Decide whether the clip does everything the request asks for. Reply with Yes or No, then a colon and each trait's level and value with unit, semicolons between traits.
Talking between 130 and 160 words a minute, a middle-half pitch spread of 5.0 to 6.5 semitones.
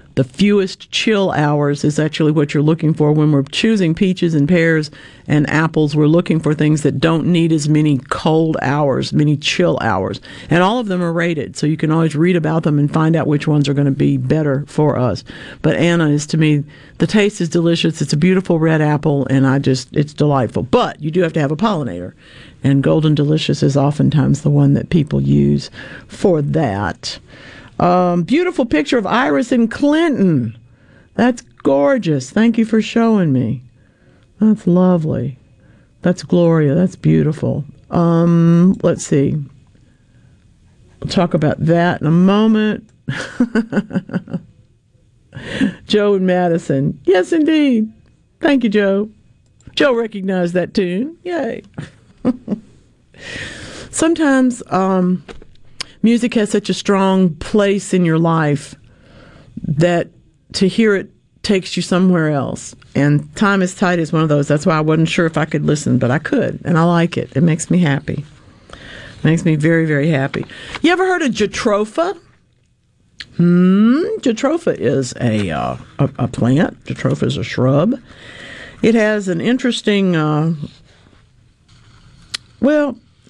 Yes: average, 155 wpm; wide, 5.6 semitones